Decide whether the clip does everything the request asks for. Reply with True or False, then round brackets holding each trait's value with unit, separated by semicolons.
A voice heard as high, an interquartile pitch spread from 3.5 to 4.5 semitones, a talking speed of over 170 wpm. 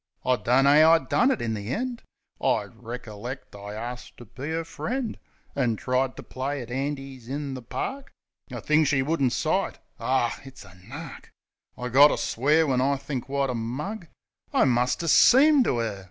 False (135 Hz; 3.9 semitones; 185 wpm)